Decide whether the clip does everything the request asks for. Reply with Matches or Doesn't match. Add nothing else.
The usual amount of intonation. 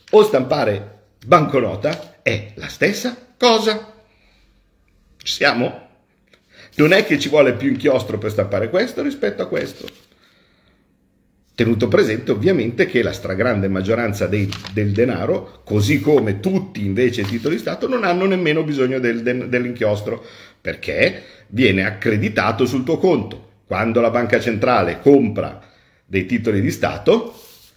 Doesn't match